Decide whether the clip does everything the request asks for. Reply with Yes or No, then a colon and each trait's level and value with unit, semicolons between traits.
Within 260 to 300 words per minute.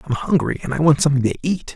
Yes: fast, 275 wpm